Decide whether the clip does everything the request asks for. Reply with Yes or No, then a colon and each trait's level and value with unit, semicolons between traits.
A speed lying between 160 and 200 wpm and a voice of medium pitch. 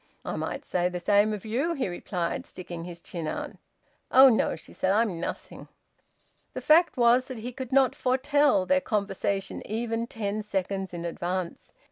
No: average, 170 wpm; high, 210 Hz